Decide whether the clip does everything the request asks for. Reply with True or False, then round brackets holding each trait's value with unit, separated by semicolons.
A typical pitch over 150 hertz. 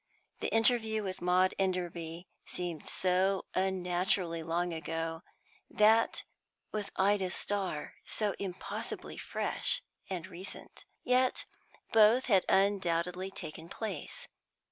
True (185 Hz)